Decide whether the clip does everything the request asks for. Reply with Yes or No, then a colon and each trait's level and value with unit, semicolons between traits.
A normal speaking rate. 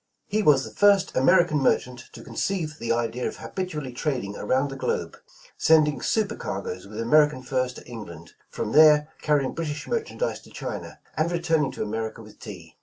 Yes: average, 180 wpm